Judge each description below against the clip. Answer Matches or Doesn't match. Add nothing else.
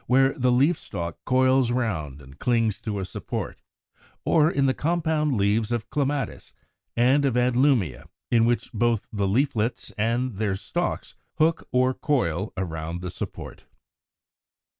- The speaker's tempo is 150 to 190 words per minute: Doesn't match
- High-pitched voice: Doesn't match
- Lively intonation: Doesn't match